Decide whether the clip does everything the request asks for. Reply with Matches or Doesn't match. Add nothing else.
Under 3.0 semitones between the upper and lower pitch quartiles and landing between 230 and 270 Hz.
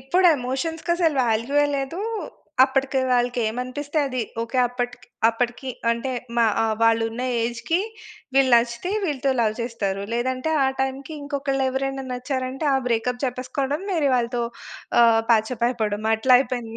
Matches